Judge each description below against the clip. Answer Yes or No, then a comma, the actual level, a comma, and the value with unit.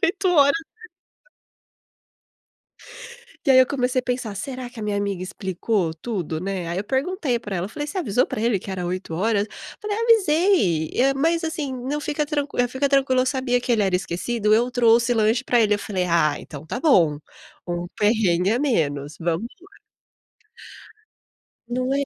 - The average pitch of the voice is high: Yes, high, 235 Hz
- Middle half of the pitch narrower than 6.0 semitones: No, wide, 6.4 semitones